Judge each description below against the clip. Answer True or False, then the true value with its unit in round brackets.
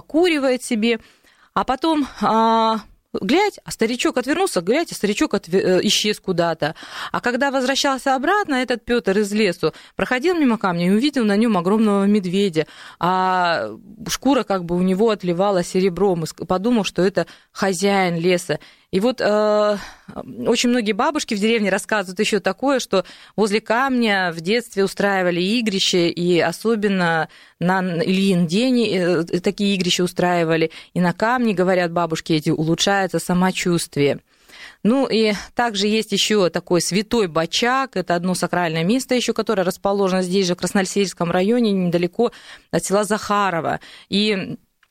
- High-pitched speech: True (200 Hz)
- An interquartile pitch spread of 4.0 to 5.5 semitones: True (4.3 semitones)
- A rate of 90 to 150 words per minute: True (140 wpm)